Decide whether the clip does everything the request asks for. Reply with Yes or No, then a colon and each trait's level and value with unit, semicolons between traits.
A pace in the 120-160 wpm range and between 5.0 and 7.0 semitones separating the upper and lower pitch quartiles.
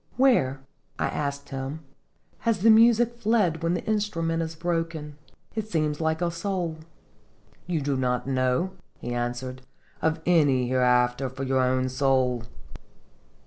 Yes: average, 140 wpm; average, 5.3 semitones